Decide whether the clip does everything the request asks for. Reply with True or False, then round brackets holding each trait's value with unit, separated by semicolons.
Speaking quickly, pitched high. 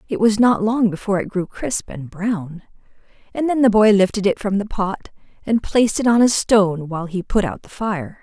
True (225 wpm; 205 Hz)